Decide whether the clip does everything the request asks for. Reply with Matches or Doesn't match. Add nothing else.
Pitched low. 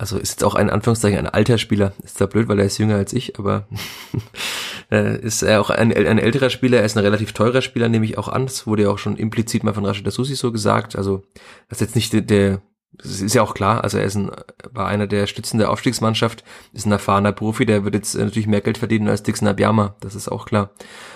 Matches